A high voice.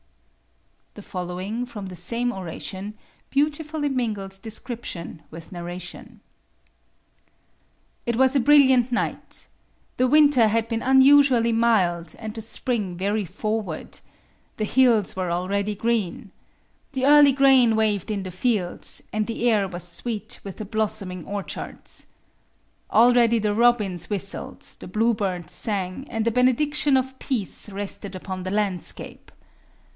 Yes: high, 220 Hz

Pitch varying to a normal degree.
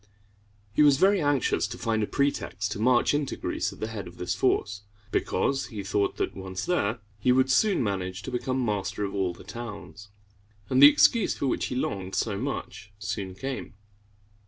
Yes: average, 4.9 semitones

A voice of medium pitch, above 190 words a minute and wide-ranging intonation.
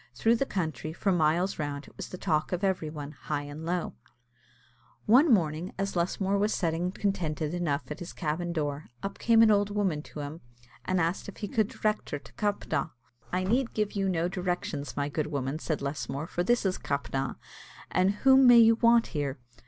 No: medium, 175 Hz; average, 200 wpm; average, 4.9 semitones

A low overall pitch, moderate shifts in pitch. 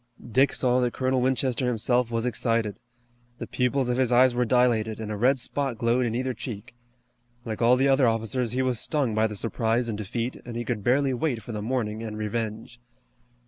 No: low, 120 Hz; narrow, 2.3 semitones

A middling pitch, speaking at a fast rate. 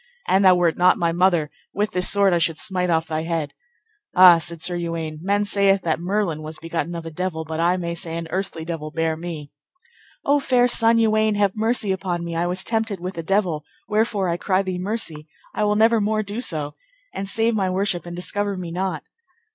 Yes: medium, 180 Hz; fast, 215 wpm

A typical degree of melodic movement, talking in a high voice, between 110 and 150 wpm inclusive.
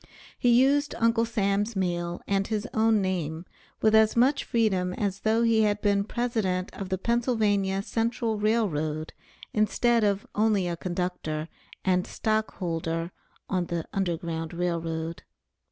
Yes: average, 4.0 semitones; high, 200 Hz; average, 145 wpm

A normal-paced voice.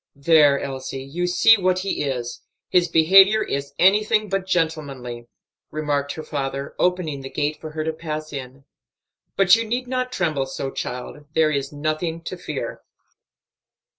Yes: average, 155 wpm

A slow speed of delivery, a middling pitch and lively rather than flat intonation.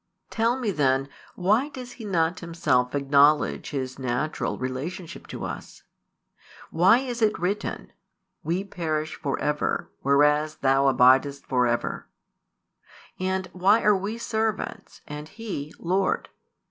Yes: slow, 125 wpm; medium, 160 Hz; wide, 6.2 semitones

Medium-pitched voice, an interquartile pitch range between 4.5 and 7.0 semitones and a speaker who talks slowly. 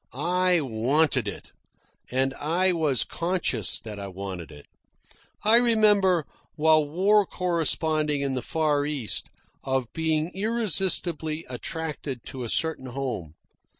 Yes: medium, 155 Hz; average, 5.3 semitones; slow, 120 wpm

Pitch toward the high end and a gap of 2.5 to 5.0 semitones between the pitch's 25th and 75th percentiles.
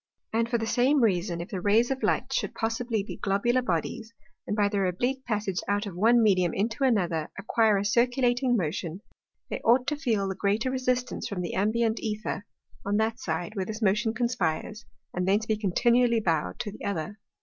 Yes: high, 215 Hz; average, 3.5 semitones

